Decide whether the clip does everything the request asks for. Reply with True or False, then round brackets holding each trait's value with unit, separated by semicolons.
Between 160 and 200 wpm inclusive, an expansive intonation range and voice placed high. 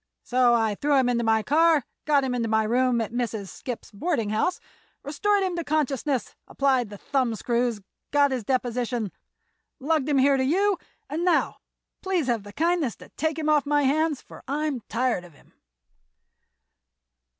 False (165 wpm; 4.4 semitones; 265 Hz)